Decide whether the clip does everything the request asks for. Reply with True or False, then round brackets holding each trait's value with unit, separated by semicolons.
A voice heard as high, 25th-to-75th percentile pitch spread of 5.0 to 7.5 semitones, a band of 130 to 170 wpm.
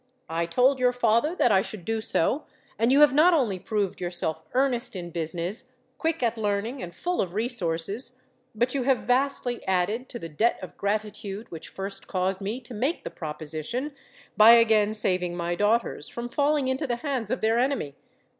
False (225 Hz; 5.4 semitones; 185 wpm)